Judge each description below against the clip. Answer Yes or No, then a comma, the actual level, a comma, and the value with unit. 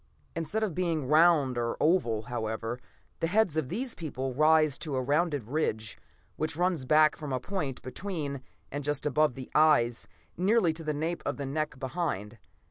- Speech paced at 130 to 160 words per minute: No, average, 175 wpm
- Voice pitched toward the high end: No, medium, 150 Hz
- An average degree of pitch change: Yes, average, 4.2 semitones